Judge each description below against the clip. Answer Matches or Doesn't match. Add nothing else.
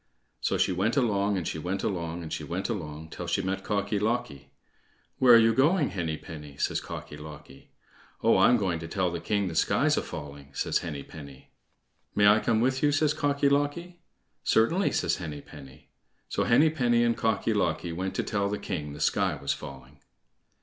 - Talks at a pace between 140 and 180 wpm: Doesn't match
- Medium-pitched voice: Doesn't match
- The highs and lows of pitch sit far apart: Matches